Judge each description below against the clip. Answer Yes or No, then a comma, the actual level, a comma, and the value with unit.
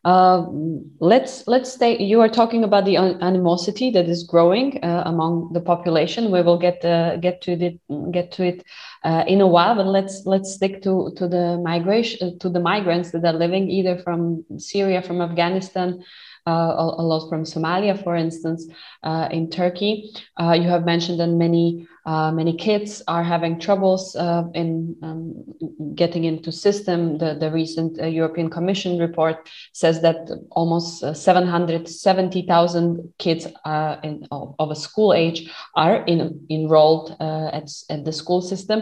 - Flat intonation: Yes, narrow, 2.1 semitones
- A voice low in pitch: No, medium, 170 Hz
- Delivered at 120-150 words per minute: No, fast, 165 wpm